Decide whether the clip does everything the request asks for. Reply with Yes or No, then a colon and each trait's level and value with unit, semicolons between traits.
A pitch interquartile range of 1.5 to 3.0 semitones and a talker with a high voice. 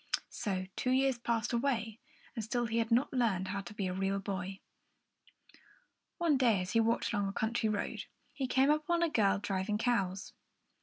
No: average, 3.9 semitones; high, 225 Hz